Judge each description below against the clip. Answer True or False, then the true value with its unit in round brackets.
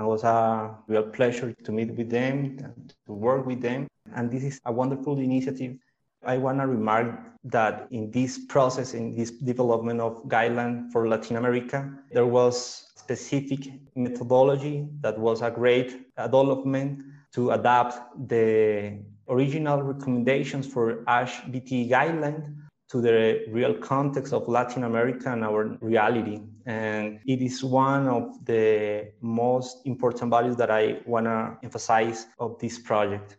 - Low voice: True (120 Hz)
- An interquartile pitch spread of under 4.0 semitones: True (2.5 semitones)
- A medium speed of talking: True (145 wpm)